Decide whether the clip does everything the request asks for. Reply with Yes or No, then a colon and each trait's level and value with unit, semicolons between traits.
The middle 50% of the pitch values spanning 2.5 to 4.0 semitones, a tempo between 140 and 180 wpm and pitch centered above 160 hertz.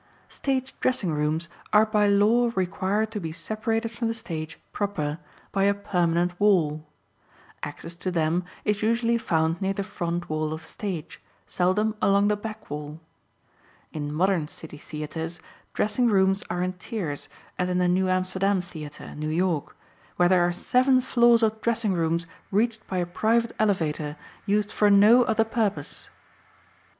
No: average, 4.6 semitones; average, 160 wpm; high, 190 Hz